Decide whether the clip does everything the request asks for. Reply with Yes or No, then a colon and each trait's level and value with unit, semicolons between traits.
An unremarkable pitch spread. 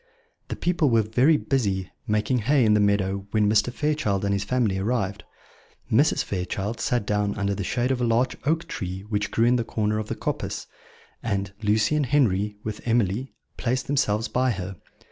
Yes: average, 3.7 semitones